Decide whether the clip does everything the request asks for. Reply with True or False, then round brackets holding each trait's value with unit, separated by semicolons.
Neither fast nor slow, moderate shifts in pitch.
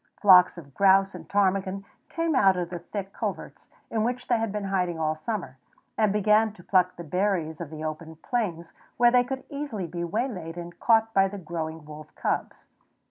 True (190 wpm; 4.3 semitones)